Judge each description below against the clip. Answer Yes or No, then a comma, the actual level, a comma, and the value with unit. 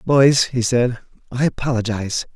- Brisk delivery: No, slow, 125 wpm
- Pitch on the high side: No, low, 125 Hz